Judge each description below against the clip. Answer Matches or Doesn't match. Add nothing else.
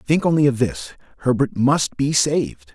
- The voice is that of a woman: Doesn't match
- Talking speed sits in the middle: Matches